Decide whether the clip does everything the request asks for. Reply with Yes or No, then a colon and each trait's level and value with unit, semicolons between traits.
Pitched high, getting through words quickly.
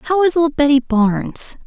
No: very high, 290 Hz; average, 180 wpm